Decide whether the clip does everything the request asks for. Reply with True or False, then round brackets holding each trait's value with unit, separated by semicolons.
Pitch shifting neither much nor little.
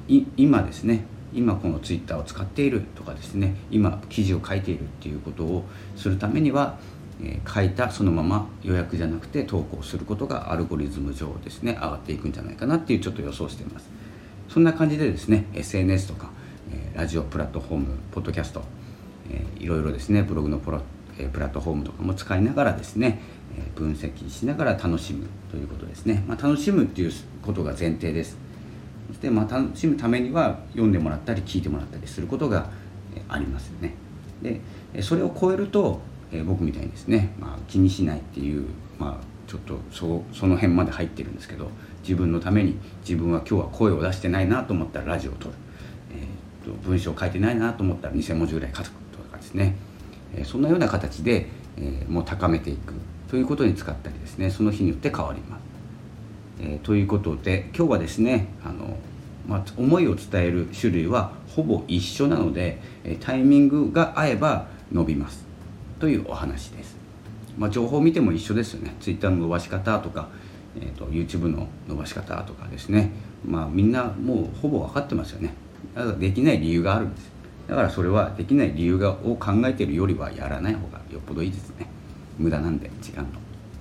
True (4.4 semitones)